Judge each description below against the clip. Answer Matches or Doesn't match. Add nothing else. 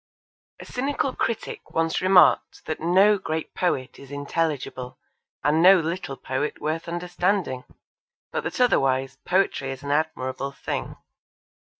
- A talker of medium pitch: Matches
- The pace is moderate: Doesn't match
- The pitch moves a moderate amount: Matches